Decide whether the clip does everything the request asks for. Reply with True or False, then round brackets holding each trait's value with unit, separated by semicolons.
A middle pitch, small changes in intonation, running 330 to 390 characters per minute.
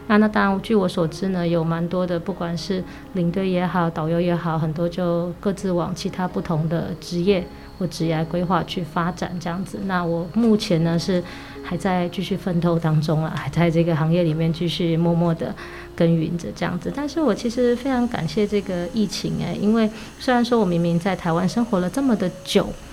False (175 Hz; 2.3 semitones; 305 characters per minute)